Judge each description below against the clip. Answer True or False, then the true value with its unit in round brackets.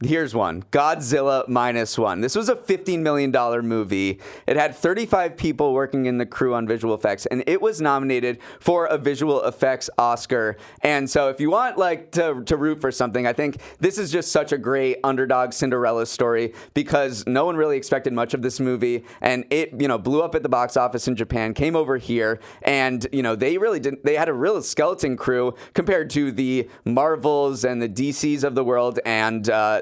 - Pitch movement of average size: True (3.5 semitones)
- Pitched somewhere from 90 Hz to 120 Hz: False (135 Hz)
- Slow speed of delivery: False (205 wpm)